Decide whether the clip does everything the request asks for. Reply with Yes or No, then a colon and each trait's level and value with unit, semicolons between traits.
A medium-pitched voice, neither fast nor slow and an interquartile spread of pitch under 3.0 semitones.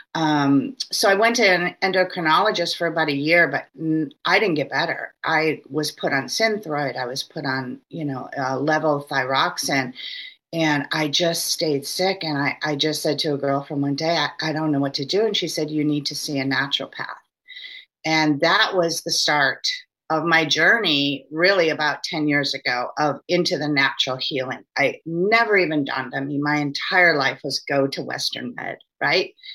No: medium, 155 Hz; average, 195 wpm; average, 3.4 semitones